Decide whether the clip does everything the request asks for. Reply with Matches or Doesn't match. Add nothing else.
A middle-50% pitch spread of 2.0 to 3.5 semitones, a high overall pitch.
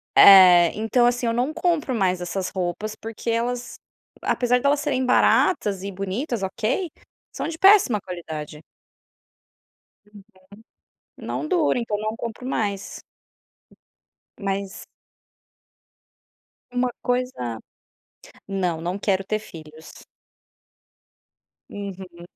Doesn't match